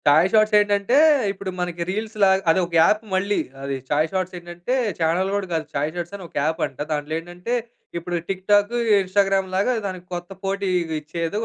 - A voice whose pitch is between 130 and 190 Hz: Yes, medium, 185 Hz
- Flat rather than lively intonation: No, average, 3.2 semitones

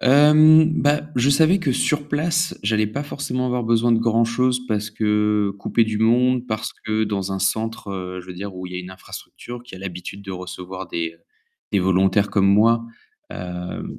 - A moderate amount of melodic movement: Yes, average, 4.8 semitones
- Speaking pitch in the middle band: No, low, 110 Hz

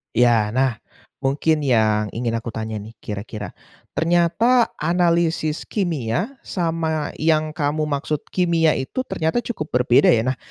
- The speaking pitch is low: No, medium, 155 Hz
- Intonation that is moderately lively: No, wide, 6.1 semitones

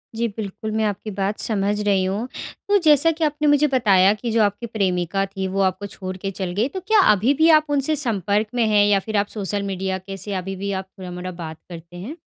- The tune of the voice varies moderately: Yes, average, 3.4 semitones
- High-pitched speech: Yes, high, 205 Hz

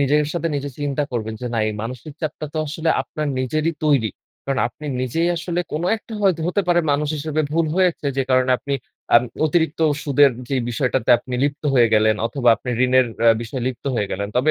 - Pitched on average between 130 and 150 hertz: Yes, medium, 140 Hz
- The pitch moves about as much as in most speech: Yes, average, 3.8 semitones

